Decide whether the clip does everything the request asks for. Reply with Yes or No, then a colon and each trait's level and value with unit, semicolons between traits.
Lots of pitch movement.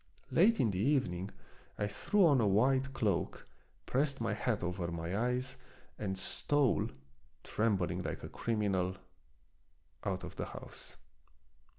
Yes: wide, 5.7 semitones